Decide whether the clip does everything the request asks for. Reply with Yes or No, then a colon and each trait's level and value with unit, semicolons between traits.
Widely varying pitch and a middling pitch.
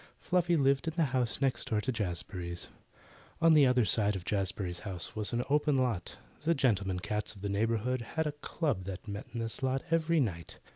No: wide, 5.9 semitones; low, 115 Hz